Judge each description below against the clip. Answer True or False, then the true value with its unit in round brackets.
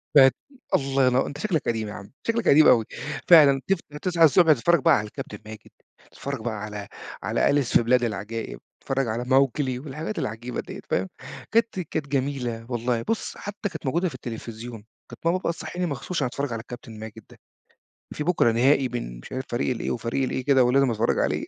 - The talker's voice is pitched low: True (130 Hz)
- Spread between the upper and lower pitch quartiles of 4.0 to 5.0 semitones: True (4.7 semitones)